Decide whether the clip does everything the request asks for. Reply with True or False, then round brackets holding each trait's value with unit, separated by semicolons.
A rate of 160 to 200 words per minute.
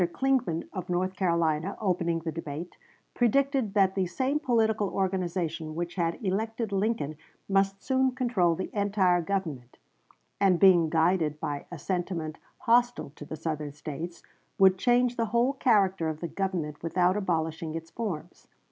False (150 wpm)